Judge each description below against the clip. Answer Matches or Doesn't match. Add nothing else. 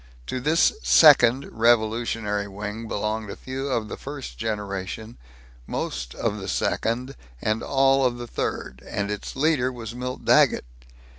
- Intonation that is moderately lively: Matches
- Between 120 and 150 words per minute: Matches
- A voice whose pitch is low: Matches